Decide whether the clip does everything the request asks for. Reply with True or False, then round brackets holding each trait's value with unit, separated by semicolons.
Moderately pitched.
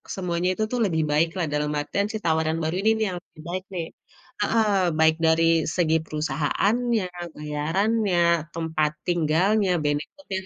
True (170 Hz)